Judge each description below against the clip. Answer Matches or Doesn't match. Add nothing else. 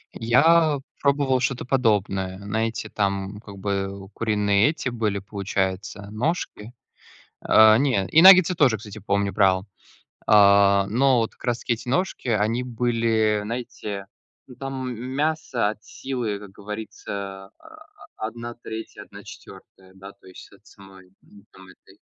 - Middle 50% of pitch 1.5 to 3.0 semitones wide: Doesn't match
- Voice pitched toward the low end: Matches